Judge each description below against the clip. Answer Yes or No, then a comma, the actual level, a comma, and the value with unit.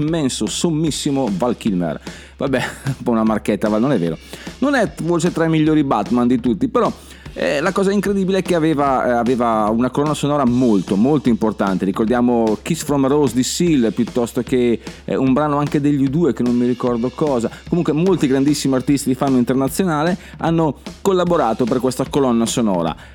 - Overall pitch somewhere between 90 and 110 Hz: No, low, 135 Hz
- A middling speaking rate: No, fast, 180 wpm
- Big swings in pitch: No, average, 4.5 semitones